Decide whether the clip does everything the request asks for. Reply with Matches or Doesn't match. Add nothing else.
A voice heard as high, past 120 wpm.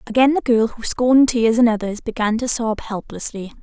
Matches